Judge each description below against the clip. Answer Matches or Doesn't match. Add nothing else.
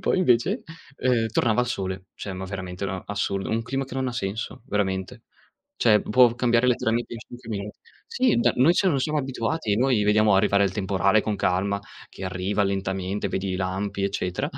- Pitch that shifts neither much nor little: Matches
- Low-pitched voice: Matches